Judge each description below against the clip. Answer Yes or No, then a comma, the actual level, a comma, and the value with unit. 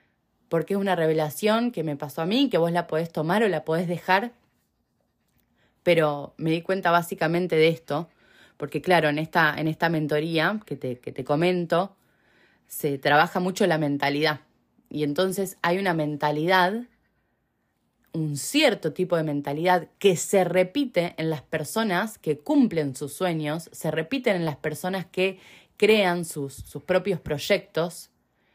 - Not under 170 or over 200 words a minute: No, average, 155 wpm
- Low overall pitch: No, medium, 165 Hz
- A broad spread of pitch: No, average, 3.5 semitones